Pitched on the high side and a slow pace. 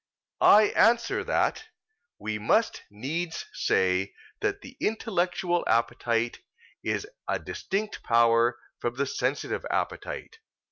No: low, 135 Hz; slow, 105 wpm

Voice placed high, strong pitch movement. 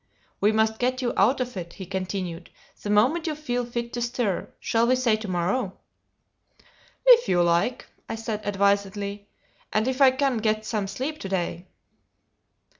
No: high, 220 Hz; average, 4.1 semitones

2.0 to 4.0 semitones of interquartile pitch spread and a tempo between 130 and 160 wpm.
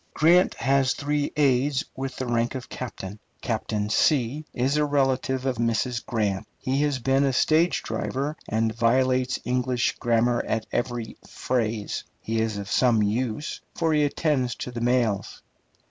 Yes: average, 2.9 semitones; average, 150 wpm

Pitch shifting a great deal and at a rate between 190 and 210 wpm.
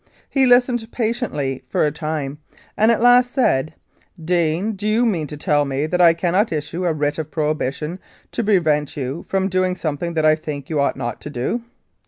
Yes: wide, 5.9 semitones; average, 195 wpm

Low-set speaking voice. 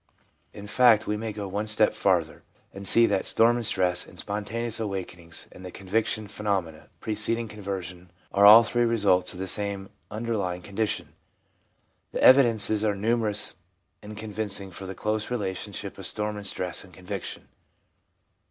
Yes: low, 105 Hz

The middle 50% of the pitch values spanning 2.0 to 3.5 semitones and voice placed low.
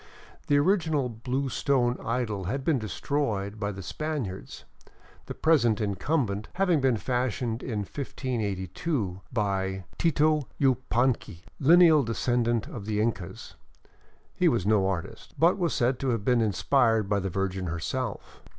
No: wide, 5.5 semitones; low, 120 Hz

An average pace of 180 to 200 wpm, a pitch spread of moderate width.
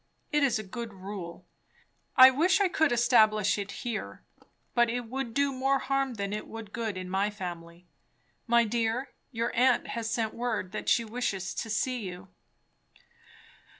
No: average, 165 wpm; average, 3.7 semitones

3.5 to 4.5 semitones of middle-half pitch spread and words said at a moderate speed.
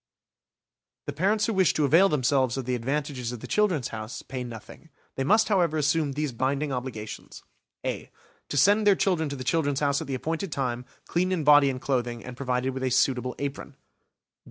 Yes: average, 4.1 semitones; average, 195 wpm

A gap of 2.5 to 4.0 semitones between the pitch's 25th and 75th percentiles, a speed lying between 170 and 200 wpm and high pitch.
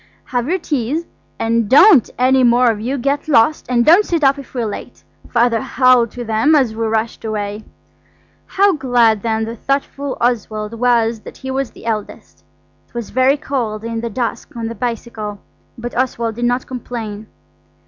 Yes: average, 2.8 semitones; average, 180 wpm; high, 240 Hz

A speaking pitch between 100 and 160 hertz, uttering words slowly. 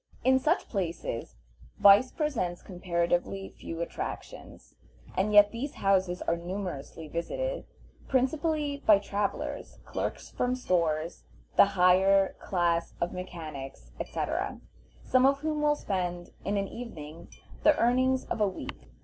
No: high, 195 Hz; slow, 125 wpm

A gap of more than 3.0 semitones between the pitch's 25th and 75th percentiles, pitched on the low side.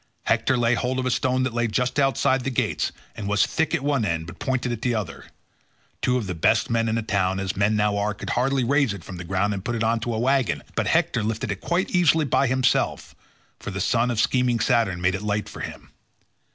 Yes: average, 4.0 semitones; low, 115 Hz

